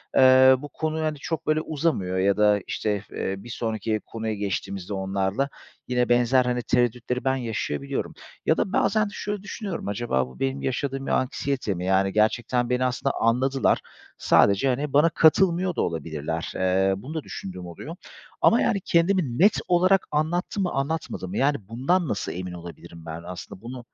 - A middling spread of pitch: No, wide, 7.5 semitones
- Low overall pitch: Yes, low, 125 Hz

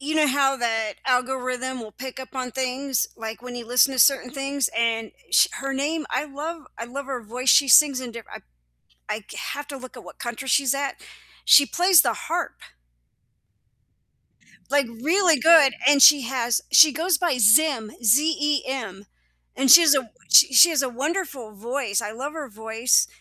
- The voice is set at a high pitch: Yes, very high, 265 Hz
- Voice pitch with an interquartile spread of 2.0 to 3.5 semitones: Yes, average, 3.2 semitones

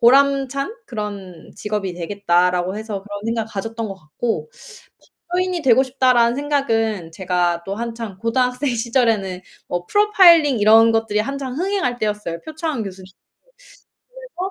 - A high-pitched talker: Yes, high, 225 Hz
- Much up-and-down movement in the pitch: Yes, wide, 5.7 semitones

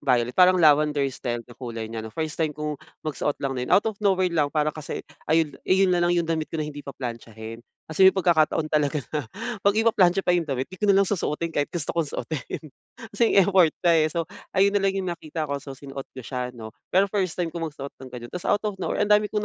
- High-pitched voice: No, medium, 155 Hz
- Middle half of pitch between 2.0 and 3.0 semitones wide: No, average, 4.6 semitones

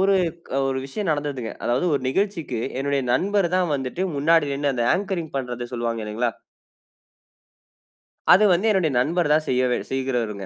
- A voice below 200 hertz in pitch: Yes, medium, 140 Hz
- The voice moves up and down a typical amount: No, wide, 6.0 semitones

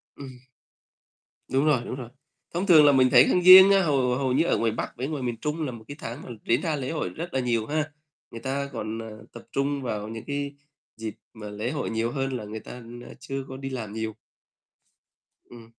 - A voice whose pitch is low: Yes, low, 130 Hz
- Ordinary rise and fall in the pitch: Yes, average, 3.9 semitones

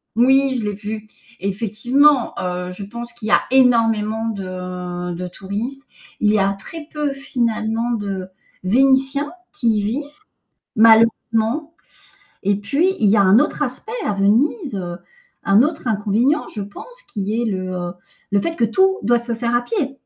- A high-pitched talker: Yes, high, 225 Hz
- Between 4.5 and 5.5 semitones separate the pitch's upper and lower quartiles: Yes, average, 5.0 semitones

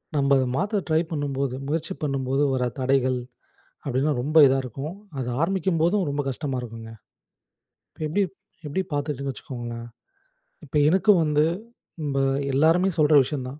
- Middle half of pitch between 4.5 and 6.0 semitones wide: No, average, 3.4 semitones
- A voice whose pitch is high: No, medium, 145 Hz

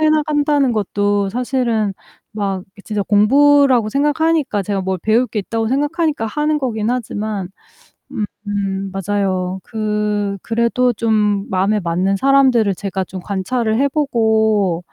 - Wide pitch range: No, average, 4.3 semitones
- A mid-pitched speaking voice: No, high, 215 Hz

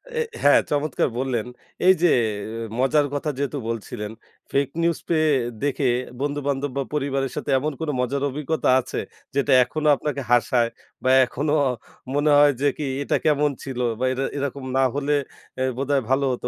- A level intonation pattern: Yes, narrow, 2.0 semitones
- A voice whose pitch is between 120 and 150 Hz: Yes, medium, 140 Hz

